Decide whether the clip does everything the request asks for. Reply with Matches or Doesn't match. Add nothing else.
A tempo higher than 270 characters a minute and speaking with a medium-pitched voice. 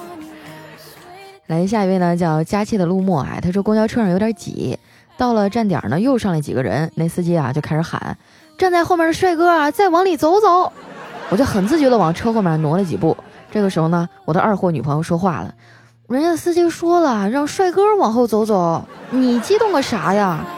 Doesn't match